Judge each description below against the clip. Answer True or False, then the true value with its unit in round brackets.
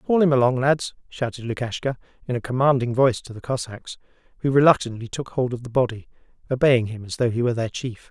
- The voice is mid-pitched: False (125 Hz)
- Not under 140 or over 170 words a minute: False (205 wpm)